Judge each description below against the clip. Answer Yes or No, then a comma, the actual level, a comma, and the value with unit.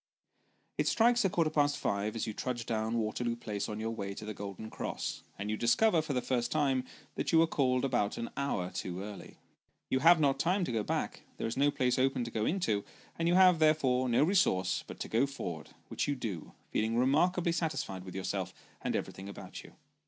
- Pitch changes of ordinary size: No, wide, 6.3 semitones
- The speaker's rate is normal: No, fast, 225 wpm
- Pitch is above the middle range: No, low, 125 Hz